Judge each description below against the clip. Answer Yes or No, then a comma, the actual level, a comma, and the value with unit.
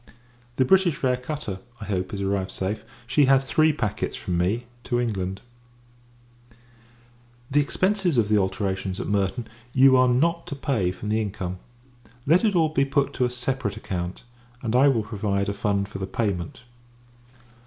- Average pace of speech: Yes, average, 170 wpm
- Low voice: Yes, low, 110 Hz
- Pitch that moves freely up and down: Yes, wide, 5.7 semitones